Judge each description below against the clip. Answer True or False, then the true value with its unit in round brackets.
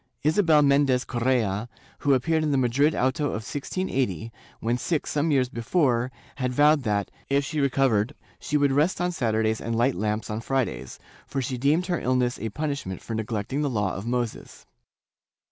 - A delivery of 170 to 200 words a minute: True (175 wpm)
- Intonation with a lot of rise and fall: False (4.2 semitones)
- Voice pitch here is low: True (130 Hz)